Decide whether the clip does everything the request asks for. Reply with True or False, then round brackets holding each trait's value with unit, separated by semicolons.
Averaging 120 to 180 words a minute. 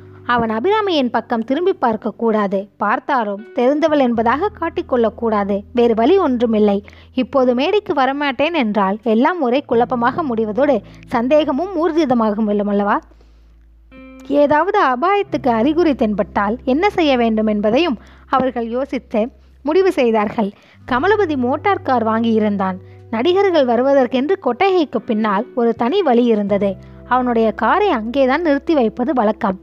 False (105 wpm)